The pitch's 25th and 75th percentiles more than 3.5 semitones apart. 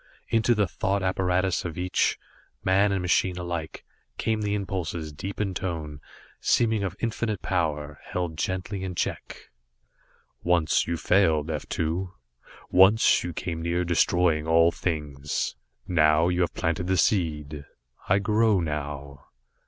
No: average, 3.2 semitones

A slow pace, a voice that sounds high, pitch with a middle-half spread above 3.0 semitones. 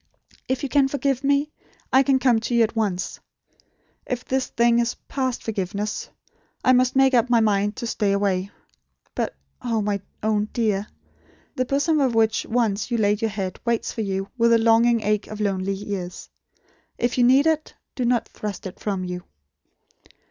No: average, 180 wpm; high, 225 Hz; average, 3.6 semitones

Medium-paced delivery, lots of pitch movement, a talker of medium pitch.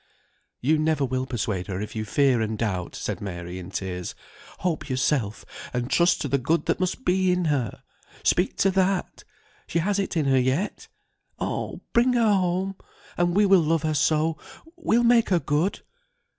Yes: average, 180 wpm; wide, 7.4 semitones; medium, 155 Hz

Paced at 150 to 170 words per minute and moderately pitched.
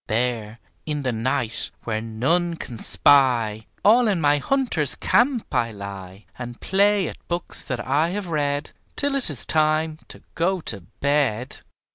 Yes: average, 155 wpm; medium, 145 Hz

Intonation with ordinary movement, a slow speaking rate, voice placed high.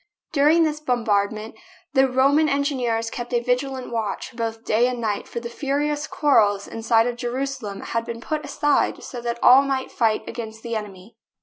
No: average, 3.4 semitones; average, 185 wpm; high, 240 Hz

